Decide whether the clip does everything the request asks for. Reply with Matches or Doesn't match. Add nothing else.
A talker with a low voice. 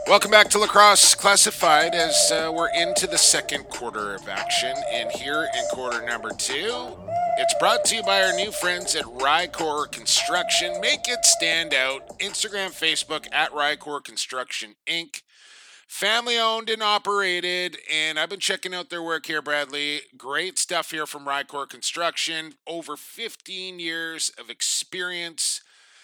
Doesn't match